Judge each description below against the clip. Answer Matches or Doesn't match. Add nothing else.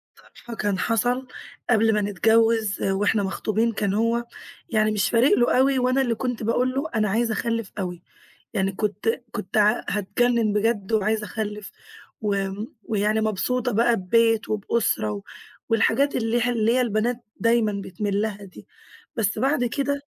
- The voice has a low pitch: Doesn't match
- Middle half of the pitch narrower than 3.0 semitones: Matches